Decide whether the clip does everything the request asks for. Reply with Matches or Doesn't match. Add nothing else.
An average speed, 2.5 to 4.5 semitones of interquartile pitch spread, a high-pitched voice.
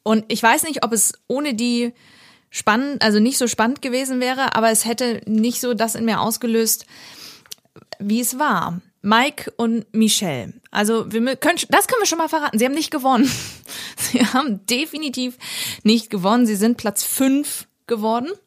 Matches